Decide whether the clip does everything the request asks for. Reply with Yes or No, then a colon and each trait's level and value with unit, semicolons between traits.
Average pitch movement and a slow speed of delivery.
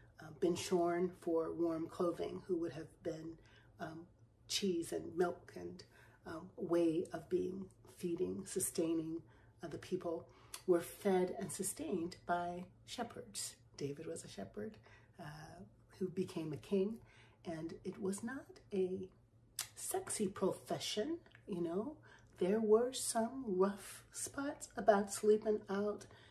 Yes: average, 3.2 semitones; slow, 130 wpm